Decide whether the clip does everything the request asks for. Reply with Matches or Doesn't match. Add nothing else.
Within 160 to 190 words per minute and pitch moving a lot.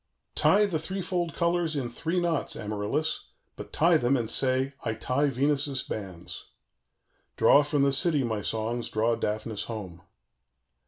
Doesn't match